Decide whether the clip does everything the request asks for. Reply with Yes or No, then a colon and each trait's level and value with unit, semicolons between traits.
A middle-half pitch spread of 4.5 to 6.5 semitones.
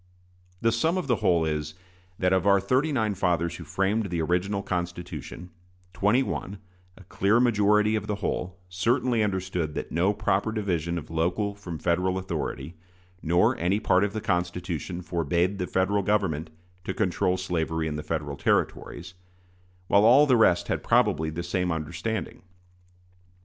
No: average, 3.5 semitones